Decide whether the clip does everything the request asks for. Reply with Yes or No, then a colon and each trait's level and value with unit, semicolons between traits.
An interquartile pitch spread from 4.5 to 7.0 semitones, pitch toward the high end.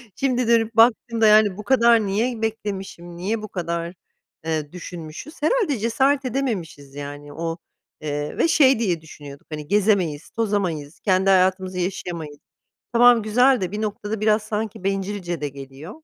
Yes: average, 5.3 semitones; high, 195 Hz